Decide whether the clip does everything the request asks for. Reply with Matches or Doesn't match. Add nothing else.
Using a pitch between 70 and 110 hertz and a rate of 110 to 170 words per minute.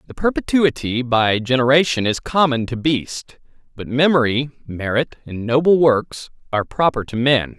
Doesn't match